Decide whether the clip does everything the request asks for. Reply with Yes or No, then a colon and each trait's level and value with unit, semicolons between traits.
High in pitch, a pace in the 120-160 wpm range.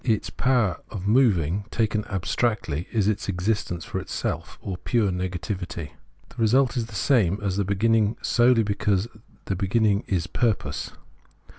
No: low, 105 Hz; average, 150 wpm